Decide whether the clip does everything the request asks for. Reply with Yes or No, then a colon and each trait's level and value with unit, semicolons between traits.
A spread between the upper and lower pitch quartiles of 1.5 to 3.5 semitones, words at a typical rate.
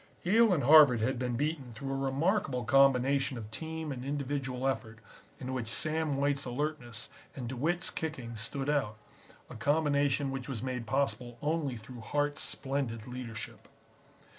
Yes: average, 3.0 semitones; average, 150 wpm